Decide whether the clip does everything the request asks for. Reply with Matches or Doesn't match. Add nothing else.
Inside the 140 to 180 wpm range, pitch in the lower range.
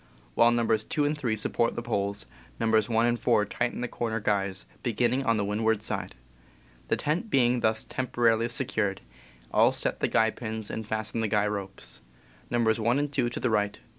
Doesn't match